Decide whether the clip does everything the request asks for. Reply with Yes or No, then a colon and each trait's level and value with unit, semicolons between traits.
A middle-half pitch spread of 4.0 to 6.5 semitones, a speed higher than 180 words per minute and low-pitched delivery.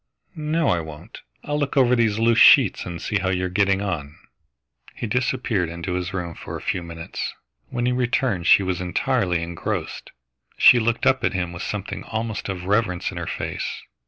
Yes: average, 5.1 semitones; average, 190 wpm; low, 100 Hz